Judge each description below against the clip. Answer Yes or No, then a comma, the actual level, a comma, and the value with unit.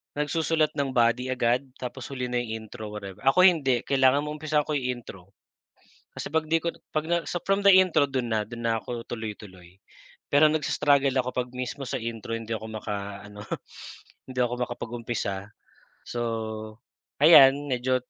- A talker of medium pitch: No, low, 125 Hz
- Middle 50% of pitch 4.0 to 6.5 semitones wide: Yes, average, 4.3 semitones